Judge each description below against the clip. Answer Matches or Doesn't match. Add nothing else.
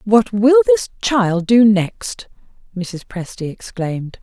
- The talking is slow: Matches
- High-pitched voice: Matches